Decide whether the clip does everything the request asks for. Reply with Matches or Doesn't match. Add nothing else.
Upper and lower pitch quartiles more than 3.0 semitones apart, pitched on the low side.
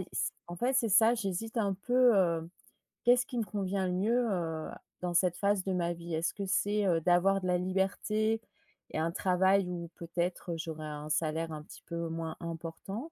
Doesn't match